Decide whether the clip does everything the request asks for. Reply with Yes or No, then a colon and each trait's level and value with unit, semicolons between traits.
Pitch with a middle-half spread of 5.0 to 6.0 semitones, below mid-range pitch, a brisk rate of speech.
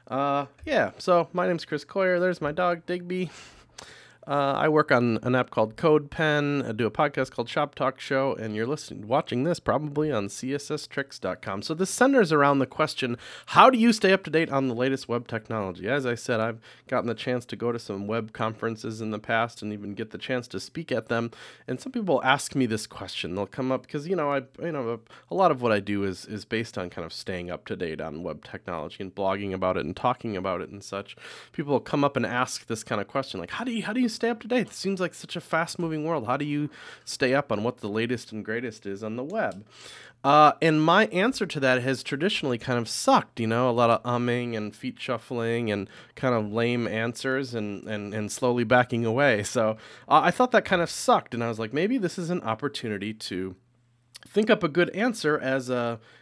Yes: average, 5.3 semitones; low, 125 Hz; fast, 240 wpm